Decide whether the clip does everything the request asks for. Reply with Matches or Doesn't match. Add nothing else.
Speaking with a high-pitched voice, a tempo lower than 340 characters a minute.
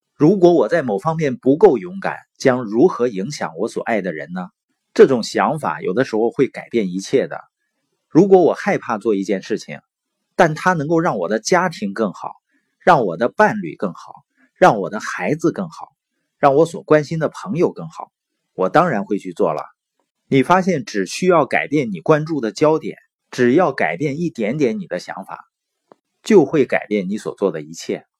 Doesn't match